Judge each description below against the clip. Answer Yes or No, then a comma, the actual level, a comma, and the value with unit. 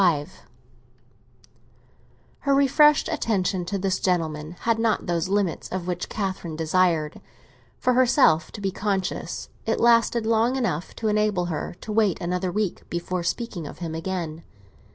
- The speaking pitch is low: No, high, 190 Hz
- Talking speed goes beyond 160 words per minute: No, average, 145 wpm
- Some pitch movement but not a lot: Yes, average, 4.5 semitones